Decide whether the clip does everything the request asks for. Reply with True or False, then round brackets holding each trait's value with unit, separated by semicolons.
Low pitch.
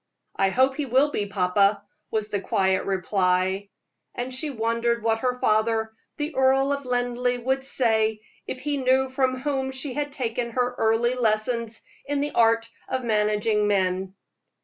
False (235 Hz)